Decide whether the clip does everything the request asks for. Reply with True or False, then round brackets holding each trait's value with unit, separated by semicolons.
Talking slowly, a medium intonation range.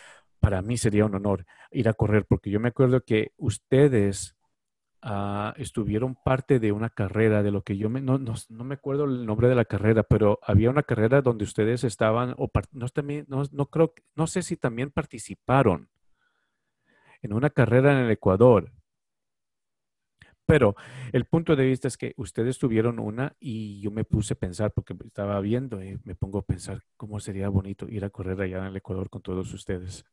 False (190 wpm; 4.2 semitones)